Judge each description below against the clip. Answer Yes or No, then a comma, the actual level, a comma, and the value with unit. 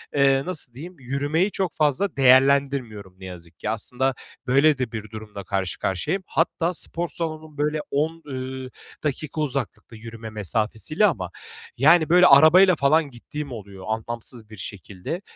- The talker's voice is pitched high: No, low, 135 Hz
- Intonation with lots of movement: Yes, wide, 6.0 semitones